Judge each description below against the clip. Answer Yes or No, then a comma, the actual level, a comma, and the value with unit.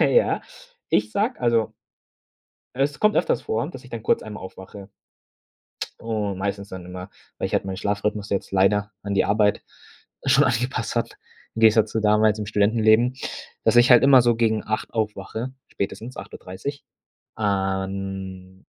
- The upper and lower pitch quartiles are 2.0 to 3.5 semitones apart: Yes, average, 2.9 semitones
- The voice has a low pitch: Yes, low, 105 Hz